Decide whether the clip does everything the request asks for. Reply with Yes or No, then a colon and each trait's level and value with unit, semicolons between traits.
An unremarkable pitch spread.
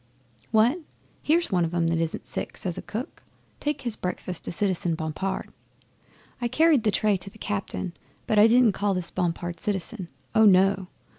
Yes: average, 3.9 semitones